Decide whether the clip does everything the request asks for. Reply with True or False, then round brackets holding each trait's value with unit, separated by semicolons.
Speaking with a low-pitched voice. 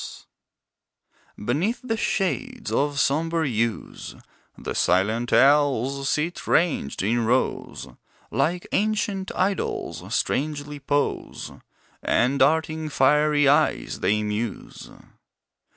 False (145 Hz)